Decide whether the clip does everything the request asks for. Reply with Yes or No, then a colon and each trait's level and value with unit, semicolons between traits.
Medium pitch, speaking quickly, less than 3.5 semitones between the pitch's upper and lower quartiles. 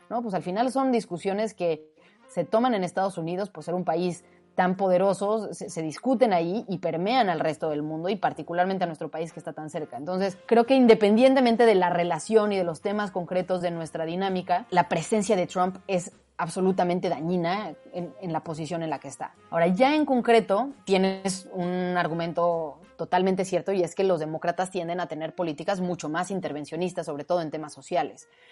Yes: medium, 180 Hz; fast, 195 wpm; average, 2.8 semitones